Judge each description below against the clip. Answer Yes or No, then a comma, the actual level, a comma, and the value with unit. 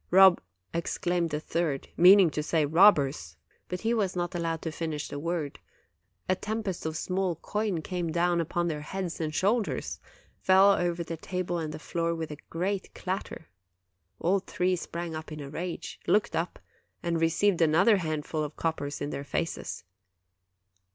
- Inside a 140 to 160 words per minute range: No, average, 170 wpm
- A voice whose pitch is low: No, medium, 170 Hz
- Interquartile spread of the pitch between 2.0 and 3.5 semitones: Yes, average, 2.7 semitones